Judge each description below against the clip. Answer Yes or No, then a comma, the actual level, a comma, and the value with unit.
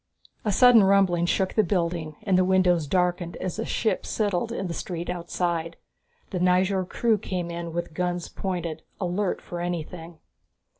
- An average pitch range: No, narrow, 1.8 semitones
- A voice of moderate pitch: Yes, medium, 180 Hz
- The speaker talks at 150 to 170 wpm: Yes, average, 160 wpm